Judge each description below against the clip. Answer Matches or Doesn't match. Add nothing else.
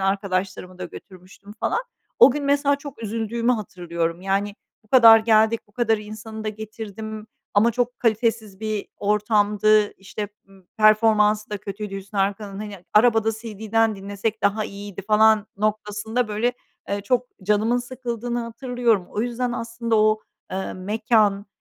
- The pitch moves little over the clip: Matches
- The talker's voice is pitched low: Doesn't match